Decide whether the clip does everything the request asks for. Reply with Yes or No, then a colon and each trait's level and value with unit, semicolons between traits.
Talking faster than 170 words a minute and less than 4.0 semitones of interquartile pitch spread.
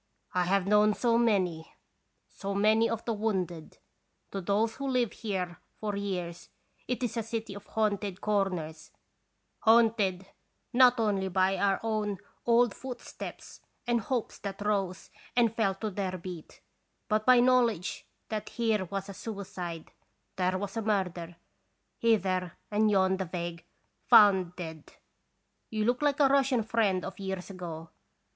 No: average, 145 wpm; average, 3.4 semitones